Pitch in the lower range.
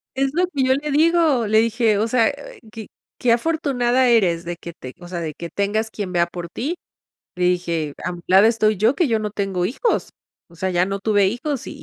No: high, 215 Hz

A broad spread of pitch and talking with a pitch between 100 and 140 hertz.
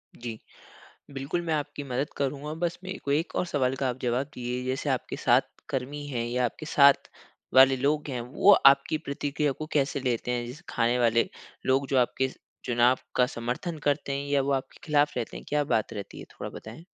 No: average, 2.8 semitones; low, 135 Hz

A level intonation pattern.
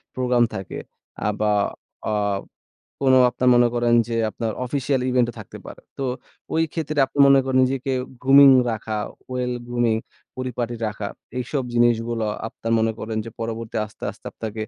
Yes: narrow, 2.2 semitones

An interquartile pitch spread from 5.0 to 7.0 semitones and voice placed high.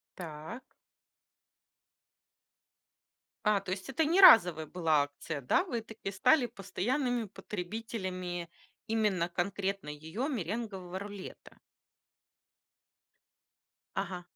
No: average, 4.3 semitones; high, 195 Hz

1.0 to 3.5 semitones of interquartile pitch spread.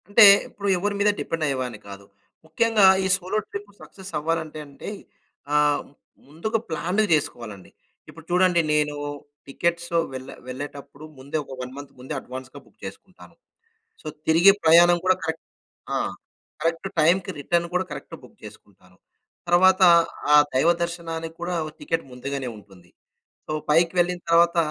No: average, 4.0 semitones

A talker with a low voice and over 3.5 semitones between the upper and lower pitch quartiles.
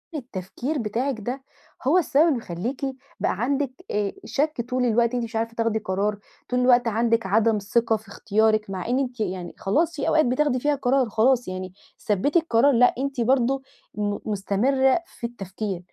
No: high, 235 Hz; average, 4.1 semitones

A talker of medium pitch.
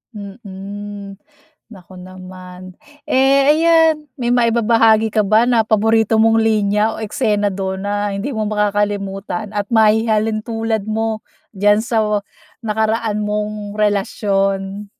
No: high, 210 Hz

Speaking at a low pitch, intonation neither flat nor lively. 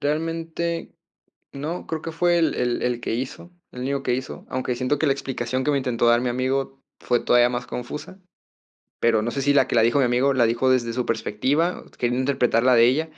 Yes: low, 130 Hz; average, 3.1 semitones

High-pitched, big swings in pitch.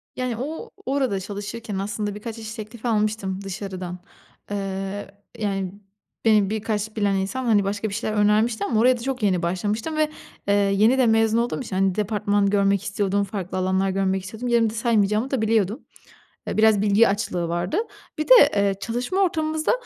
No: high, 210 Hz; average, 2.7 semitones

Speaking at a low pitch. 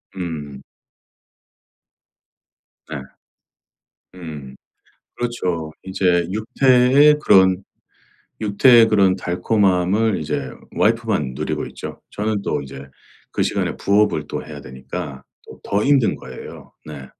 Yes: very low, 95 Hz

